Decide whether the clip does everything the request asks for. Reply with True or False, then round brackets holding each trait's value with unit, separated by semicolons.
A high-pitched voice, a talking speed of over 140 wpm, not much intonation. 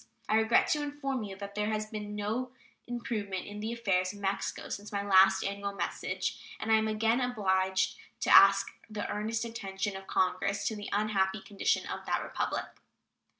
True (205 Hz; 180 wpm; 2.1 semitones)